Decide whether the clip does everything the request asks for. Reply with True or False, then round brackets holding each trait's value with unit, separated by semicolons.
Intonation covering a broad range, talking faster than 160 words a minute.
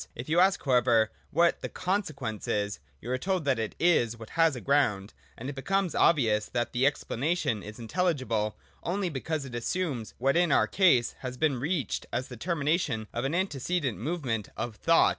True (6.4 semitones; 190 wpm)